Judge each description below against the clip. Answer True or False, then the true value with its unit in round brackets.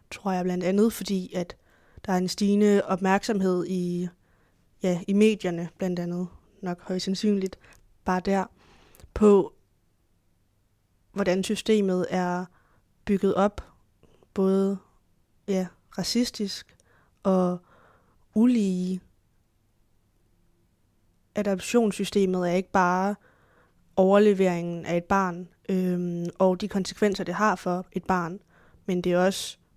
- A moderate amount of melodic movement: False (2.0 semitones)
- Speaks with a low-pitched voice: False (185 Hz)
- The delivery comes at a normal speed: False (110 wpm)